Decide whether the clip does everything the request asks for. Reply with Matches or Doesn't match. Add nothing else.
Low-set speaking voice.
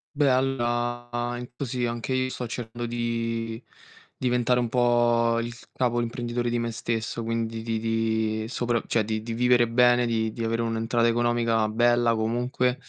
Matches